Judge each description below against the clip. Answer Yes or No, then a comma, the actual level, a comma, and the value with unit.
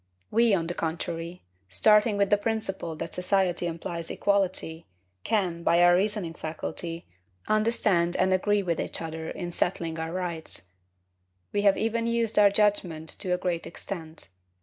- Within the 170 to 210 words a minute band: No, average, 150 wpm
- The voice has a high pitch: No, medium, 180 Hz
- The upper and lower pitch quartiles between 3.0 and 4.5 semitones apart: Yes, average, 3.6 semitones